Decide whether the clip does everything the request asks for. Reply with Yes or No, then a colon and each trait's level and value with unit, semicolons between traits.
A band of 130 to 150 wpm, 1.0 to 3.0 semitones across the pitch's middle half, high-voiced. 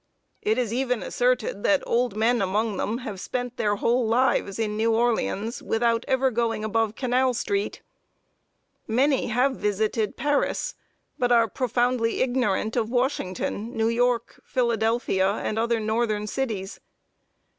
Yes: slow, 135 wpm; narrow, 2.4 semitones; high, 230 Hz